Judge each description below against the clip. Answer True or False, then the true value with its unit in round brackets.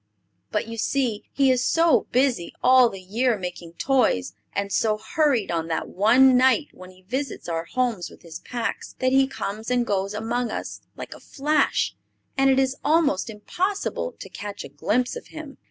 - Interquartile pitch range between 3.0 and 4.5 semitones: False (5.2 semitones)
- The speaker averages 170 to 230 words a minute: True (185 wpm)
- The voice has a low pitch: False (240 Hz)